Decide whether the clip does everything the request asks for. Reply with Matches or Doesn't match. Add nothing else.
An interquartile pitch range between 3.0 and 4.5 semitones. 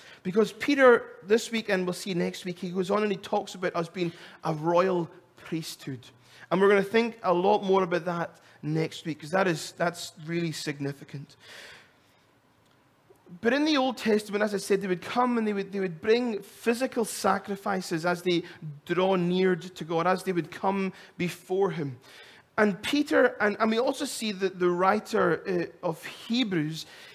Matches